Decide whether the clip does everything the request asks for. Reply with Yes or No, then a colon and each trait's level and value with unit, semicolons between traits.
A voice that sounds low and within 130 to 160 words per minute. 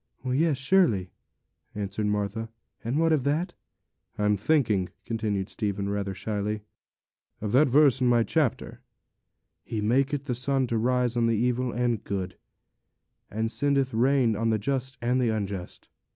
Yes: low, 115 Hz; average, 150 wpm